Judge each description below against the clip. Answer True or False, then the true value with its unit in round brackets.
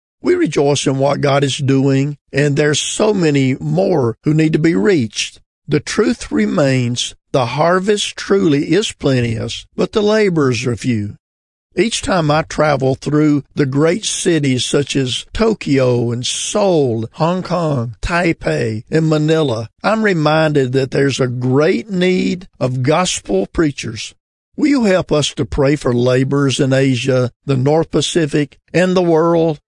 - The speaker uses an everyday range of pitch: True (4.4 semitones)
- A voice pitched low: False (145 Hz)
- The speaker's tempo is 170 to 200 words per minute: False (150 wpm)